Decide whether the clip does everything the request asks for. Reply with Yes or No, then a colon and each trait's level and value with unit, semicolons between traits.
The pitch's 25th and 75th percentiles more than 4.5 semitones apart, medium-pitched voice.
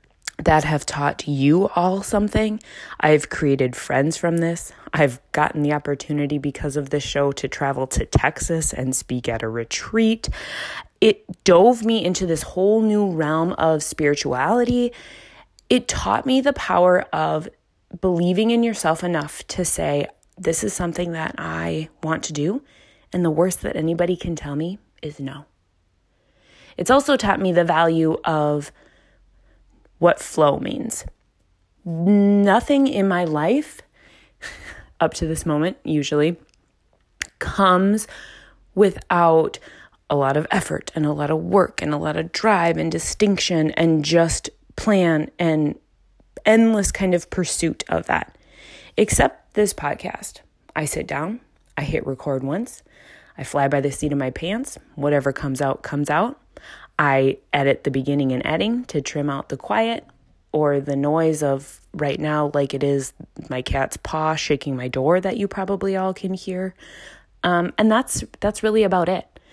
Yes: average, 4.9 semitones; medium, 160 Hz